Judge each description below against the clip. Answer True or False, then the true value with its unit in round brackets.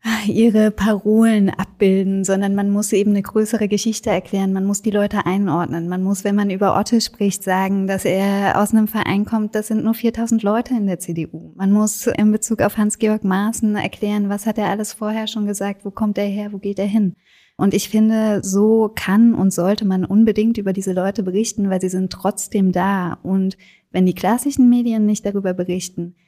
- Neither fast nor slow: False (200 wpm)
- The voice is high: True (205 Hz)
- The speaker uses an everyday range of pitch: False (2.0 semitones)